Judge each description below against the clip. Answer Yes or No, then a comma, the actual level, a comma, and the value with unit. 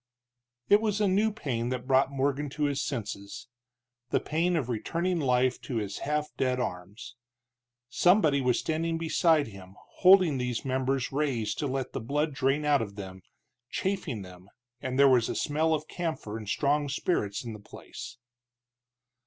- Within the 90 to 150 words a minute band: No, average, 165 wpm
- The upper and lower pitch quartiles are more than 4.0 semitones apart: Yes, average, 4.8 semitones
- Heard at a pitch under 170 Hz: Yes, low, 135 Hz